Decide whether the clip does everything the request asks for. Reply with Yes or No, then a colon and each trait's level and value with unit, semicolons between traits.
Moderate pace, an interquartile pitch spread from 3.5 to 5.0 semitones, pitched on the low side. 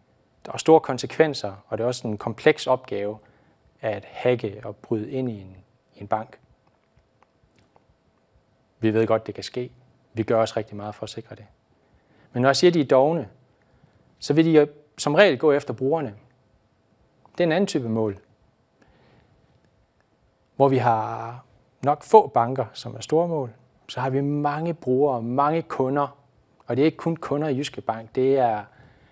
Yes: average, 175 wpm; average, 4.6 semitones; low, 130 Hz